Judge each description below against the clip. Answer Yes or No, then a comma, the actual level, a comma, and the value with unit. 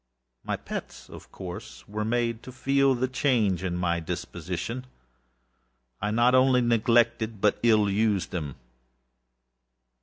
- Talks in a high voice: No, low, 110 Hz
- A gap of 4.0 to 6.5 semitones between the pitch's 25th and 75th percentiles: Yes, average, 4.5 semitones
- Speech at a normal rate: No, slow, 125 wpm